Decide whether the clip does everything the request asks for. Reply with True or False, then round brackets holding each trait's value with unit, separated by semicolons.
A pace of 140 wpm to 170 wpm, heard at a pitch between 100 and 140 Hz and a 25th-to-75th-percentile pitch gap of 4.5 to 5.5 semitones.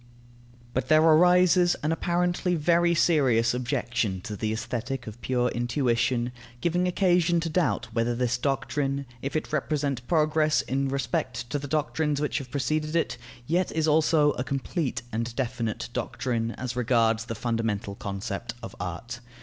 True (150 wpm; 135 Hz; 4.8 semitones)